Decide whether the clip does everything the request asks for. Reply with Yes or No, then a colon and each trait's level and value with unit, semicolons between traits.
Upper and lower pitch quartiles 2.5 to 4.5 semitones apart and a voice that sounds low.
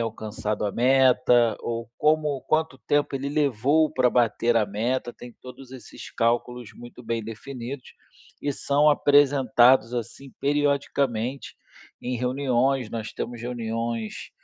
Yes: average, 2.9 semitones; low, 125 Hz